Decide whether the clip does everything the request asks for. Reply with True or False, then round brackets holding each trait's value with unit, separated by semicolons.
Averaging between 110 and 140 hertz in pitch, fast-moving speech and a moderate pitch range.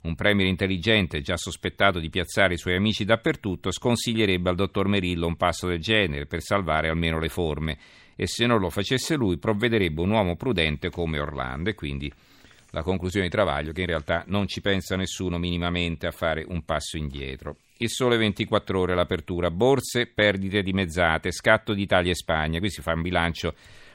False (90 Hz; 185 wpm; 3.7 semitones)